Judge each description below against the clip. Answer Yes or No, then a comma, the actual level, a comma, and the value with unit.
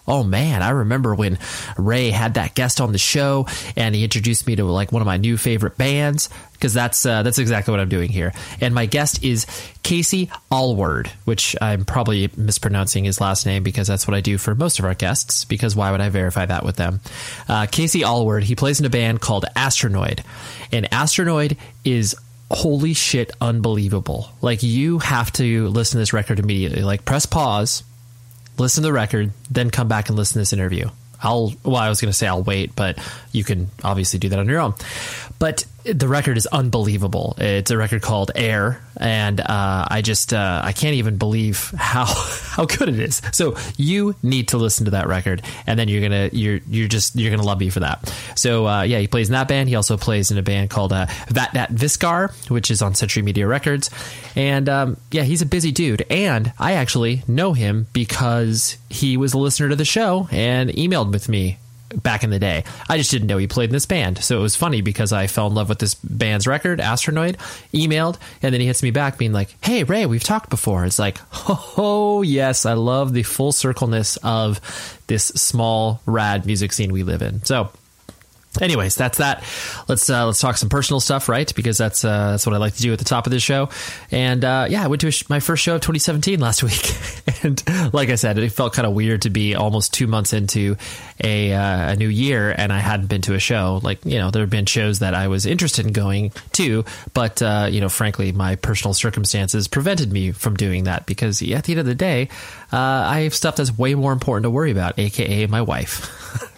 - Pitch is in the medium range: No, low, 115 Hz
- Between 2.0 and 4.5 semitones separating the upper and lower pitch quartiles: Yes, average, 4.2 semitones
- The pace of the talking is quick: Yes, fast, 220 wpm